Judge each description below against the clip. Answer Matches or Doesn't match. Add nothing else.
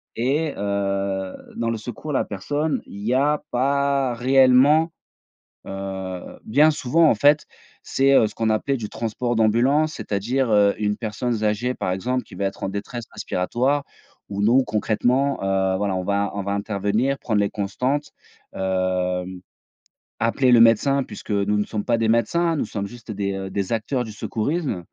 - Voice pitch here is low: Matches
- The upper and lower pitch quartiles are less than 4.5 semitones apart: Doesn't match